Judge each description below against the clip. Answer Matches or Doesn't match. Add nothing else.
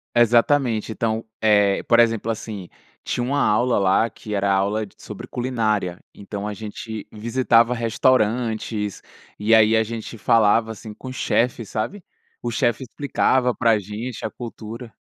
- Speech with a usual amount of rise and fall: Doesn't match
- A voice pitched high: Doesn't match